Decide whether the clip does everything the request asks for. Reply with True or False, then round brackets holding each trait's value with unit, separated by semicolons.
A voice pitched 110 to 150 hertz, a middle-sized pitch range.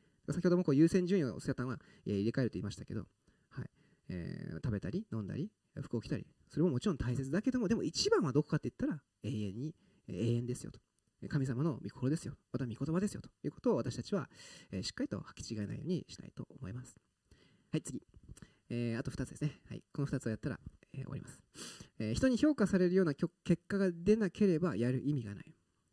False (140 Hz; 7.5 semitones)